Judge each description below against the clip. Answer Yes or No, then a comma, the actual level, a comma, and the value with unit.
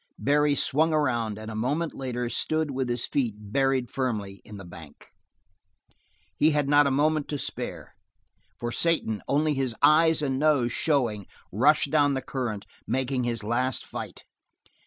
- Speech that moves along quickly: No, average, 160 wpm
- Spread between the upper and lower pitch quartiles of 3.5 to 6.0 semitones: Yes, average, 3.9 semitones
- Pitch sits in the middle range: No, low, 130 Hz